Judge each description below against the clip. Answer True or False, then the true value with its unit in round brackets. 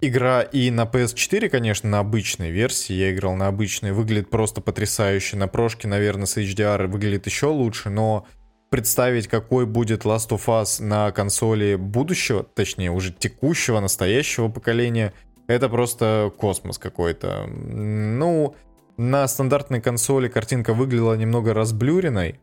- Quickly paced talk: False (135 wpm)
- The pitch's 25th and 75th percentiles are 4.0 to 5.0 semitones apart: False (3.3 semitones)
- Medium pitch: False (110 Hz)